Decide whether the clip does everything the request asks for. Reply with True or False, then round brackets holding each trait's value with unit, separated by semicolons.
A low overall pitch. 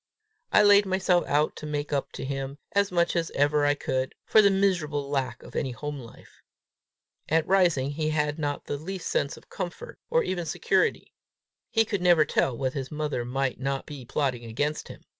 False (150 Hz)